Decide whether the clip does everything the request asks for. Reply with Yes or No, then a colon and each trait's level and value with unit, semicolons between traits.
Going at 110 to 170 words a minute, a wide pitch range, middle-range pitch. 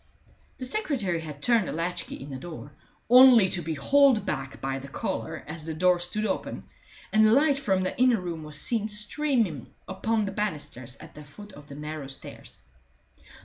No: average, 190 wpm; wide, 6.6 semitones; medium, 180 Hz